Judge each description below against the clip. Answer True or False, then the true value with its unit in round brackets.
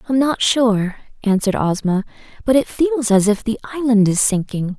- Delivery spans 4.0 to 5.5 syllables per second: True (5.1 syllables/s)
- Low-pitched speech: False (225 Hz)